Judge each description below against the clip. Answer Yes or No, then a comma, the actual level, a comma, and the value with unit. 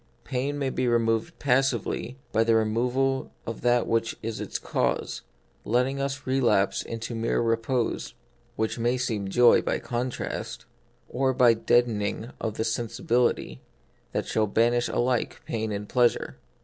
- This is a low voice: Yes, low, 120 Hz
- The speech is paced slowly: No, average, 145 wpm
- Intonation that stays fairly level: Yes, narrow, 2.1 semitones